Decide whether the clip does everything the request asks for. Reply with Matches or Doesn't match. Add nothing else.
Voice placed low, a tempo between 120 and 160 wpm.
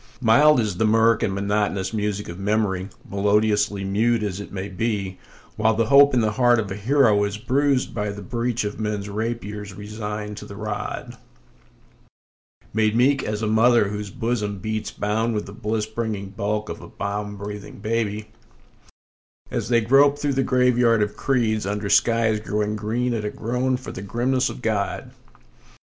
Doesn't match